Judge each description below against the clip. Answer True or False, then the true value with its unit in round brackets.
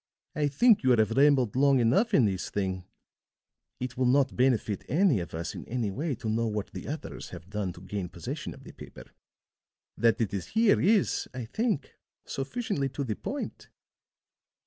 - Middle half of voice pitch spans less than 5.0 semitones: False (5.4 semitones)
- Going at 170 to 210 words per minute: True (180 wpm)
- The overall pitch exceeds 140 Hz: False (125 Hz)